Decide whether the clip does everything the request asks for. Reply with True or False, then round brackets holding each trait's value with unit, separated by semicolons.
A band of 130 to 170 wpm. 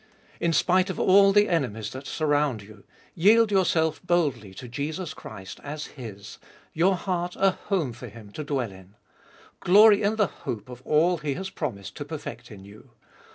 False (190 wpm)